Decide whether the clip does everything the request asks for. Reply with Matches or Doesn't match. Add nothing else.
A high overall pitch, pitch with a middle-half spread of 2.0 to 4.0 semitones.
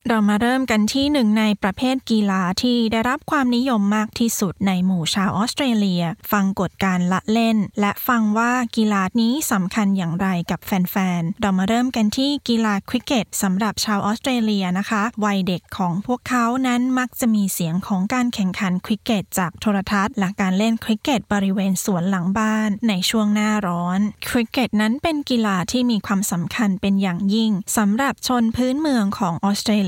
Matches